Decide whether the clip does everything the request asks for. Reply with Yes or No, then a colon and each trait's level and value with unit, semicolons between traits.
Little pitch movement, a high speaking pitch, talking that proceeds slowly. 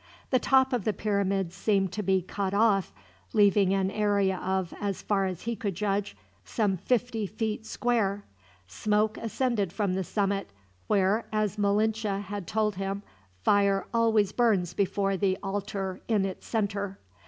No: narrow, 1.8 semitones; high, 200 Hz; average, 155 wpm